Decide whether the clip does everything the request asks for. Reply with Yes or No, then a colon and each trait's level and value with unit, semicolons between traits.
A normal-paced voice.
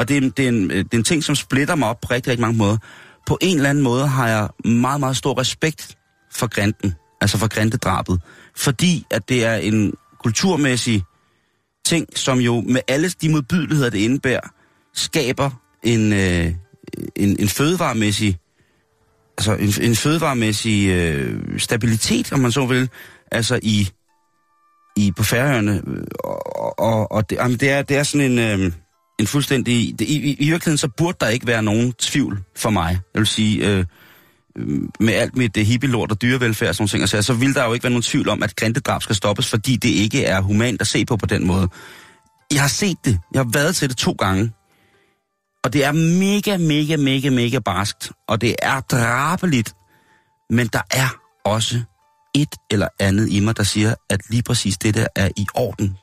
Yes: average, 185 wpm